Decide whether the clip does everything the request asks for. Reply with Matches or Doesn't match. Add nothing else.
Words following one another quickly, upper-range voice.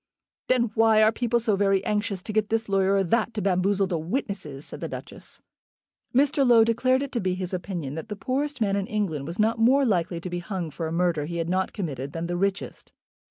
Matches